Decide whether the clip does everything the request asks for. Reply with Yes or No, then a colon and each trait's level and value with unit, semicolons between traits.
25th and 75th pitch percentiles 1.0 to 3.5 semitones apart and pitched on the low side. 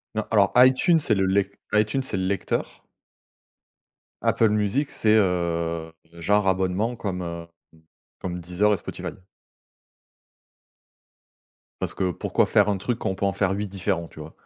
Yes: average, 2.9 semitones; low, 100 Hz